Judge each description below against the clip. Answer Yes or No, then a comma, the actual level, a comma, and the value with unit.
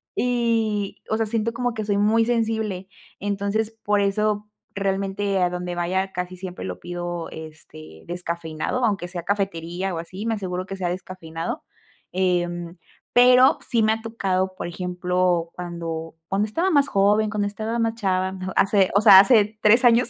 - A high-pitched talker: Yes, high, 195 Hz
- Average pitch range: Yes, average, 3.5 semitones